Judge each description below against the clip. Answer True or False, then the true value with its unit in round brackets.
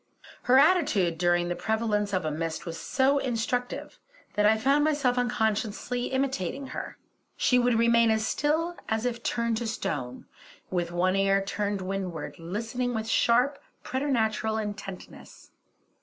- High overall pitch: True (220 Hz)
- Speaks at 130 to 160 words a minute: True (140 wpm)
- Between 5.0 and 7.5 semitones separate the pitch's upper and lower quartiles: False (4.3 semitones)